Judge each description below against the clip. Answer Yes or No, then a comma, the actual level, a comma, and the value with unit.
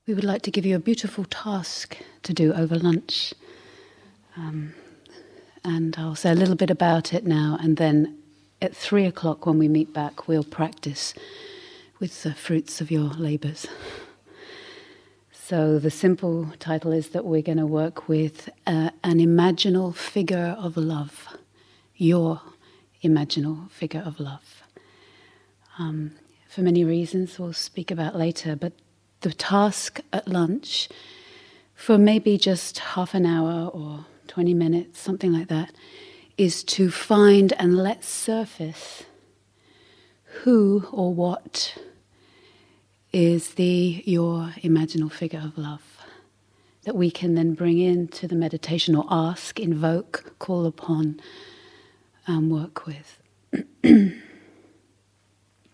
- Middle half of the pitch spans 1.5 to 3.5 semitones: No, average, 4.0 semitones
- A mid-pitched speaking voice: Yes, medium, 170 Hz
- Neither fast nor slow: No, slow, 130 wpm